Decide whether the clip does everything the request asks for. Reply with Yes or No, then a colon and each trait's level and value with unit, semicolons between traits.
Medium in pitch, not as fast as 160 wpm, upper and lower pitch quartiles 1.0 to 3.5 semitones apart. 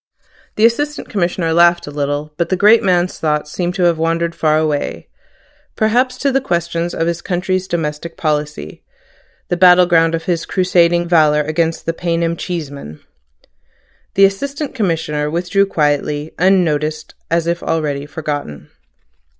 Yes: medium, 170 Hz; average, 145 wpm; average, 2.9 semitones